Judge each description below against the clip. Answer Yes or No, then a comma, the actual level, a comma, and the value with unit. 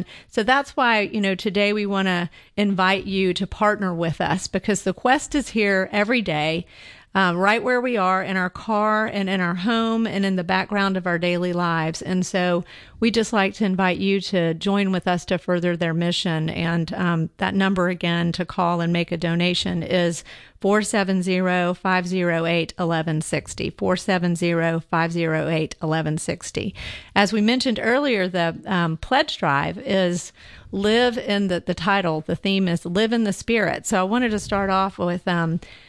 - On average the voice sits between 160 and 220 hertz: Yes, medium, 185 Hz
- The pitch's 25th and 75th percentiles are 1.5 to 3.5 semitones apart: Yes, average, 2.9 semitones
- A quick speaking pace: No, average, 175 wpm